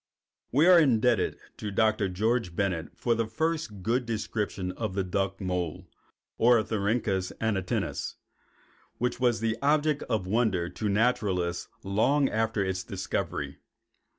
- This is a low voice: Yes, low, 110 Hz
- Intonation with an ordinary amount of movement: Yes, average, 4.1 semitones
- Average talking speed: No, slow, 125 wpm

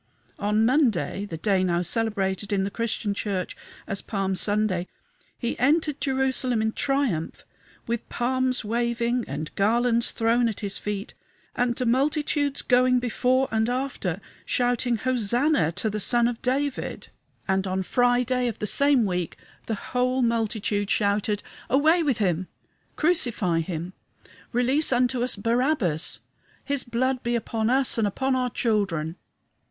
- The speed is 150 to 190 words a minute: No, average, 140 wpm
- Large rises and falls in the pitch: No, average, 4.0 semitones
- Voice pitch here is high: Yes, high, 235 Hz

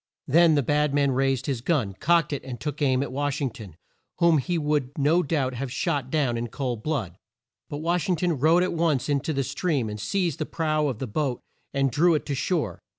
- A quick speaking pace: Yes, fast, 230 wpm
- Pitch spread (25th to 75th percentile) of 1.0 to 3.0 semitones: No, average, 3.5 semitones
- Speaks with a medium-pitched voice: Yes, medium, 145 Hz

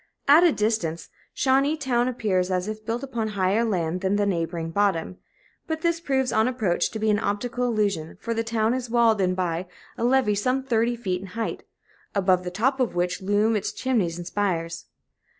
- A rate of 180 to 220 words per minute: Yes, average, 190 wpm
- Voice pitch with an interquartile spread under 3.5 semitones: No, average, 4.8 semitones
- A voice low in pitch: No, high, 215 Hz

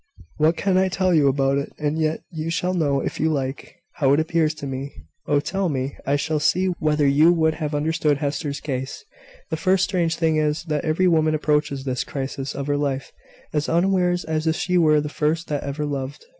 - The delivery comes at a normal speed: No, fast, 210 wpm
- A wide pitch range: No, narrow, 2.6 semitones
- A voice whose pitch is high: No, medium, 155 Hz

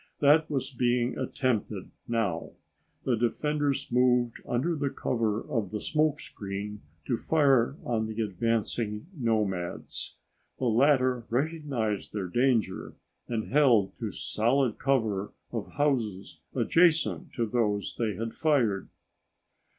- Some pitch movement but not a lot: Yes, average, 4.3 semitones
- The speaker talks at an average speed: No, slow, 115 wpm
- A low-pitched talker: Yes, low, 120 Hz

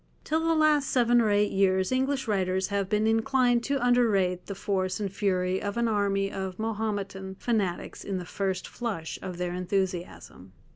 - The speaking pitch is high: Yes, high, 200 Hz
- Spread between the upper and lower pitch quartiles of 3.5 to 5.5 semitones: Yes, average, 3.9 semitones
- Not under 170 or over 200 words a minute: Yes, average, 175 wpm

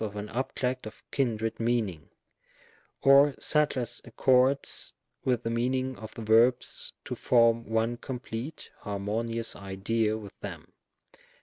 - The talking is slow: Yes, slow, 130 wpm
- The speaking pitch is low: Yes, low, 115 Hz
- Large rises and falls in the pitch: No, average, 2.8 semitones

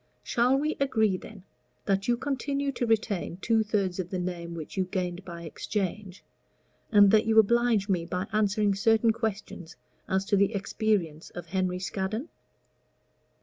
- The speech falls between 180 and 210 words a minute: No, average, 155 wpm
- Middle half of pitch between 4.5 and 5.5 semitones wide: No, average, 3.4 semitones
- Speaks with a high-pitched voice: Yes, high, 200 Hz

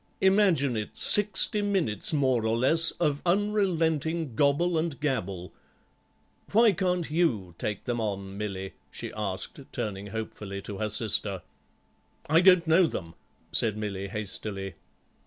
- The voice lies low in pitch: Yes, low, 130 Hz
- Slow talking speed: Yes, slow, 130 wpm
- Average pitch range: No, wide, 8.7 semitones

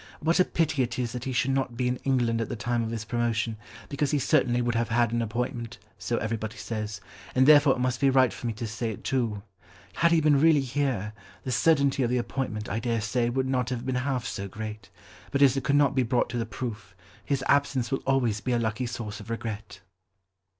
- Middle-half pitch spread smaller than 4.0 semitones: Yes, average, 2.8 semitones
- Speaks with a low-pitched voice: Yes, low, 120 Hz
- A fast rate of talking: Yes, fast, 235 wpm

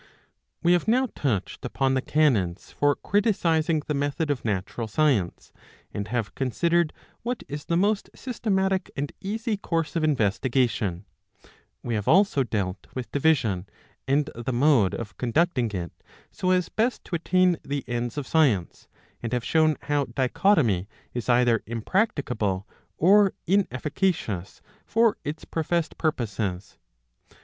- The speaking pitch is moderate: Yes, medium, 145 Hz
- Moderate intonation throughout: No, wide, 7.0 semitones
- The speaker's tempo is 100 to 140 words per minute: Yes, slow, 135 wpm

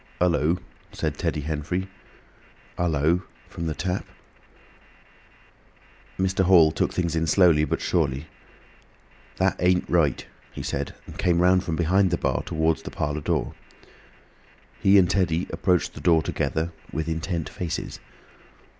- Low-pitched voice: Yes, very low, 85 Hz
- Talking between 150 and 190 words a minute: No, average, 140 wpm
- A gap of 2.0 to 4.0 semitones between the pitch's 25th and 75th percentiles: Yes, narrow, 2.4 semitones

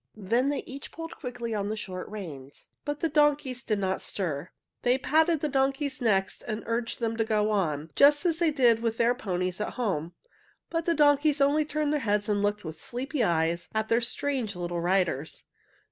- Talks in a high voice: Yes, high, 230 Hz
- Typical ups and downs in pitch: No, wide, 6.7 semitones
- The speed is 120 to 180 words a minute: No, average, 195 wpm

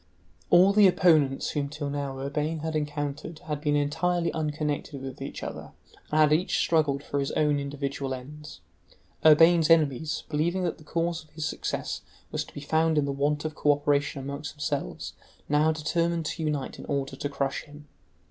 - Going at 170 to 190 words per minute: Yes, average, 175 wpm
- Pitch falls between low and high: Yes, medium, 150 Hz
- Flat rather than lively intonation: Yes, narrow, 2.0 semitones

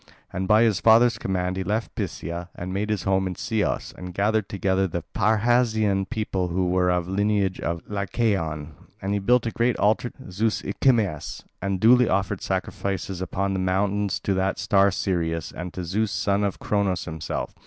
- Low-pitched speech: Yes, very low, 95 Hz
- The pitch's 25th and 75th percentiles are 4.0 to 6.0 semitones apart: No, average, 2.7 semitones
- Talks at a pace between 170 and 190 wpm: Yes, average, 185 wpm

